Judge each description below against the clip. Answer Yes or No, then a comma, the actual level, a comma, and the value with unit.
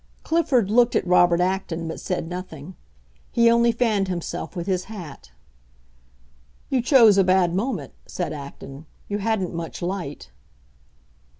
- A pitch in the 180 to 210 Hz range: Yes, medium, 185 Hz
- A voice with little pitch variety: No, average, 4.5 semitones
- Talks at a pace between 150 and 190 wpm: No, slow, 135 wpm